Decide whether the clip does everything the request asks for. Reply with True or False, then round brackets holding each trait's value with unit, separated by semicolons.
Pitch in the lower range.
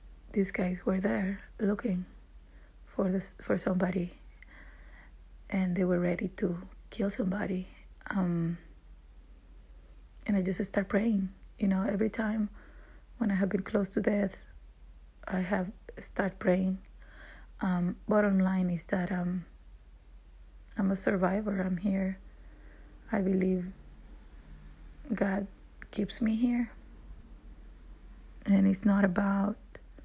False (190 Hz)